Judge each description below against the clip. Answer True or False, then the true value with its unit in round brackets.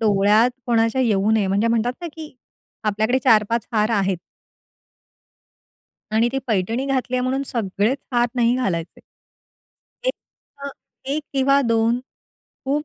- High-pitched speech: True (230 Hz)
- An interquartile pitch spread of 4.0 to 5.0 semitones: False (3.4 semitones)